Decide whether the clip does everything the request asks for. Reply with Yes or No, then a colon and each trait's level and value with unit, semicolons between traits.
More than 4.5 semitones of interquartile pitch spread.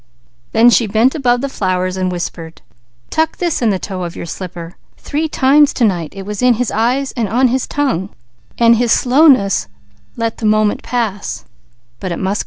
Yes: average, 5.3 semitones